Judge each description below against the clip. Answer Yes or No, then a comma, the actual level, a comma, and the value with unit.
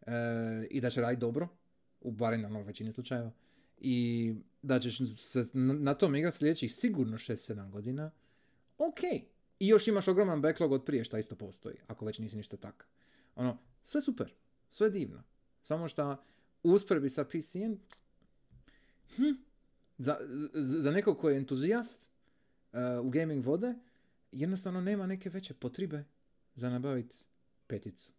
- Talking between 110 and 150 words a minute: Yes, average, 140 wpm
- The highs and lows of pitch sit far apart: Yes, wide, 8.3 semitones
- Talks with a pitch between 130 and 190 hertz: Yes, low, 135 Hz